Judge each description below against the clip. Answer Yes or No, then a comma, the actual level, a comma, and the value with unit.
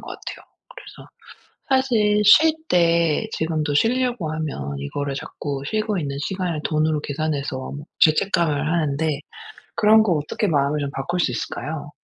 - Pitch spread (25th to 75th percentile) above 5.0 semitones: Yes, wide, 5.5 semitones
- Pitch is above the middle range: No, medium, 155 Hz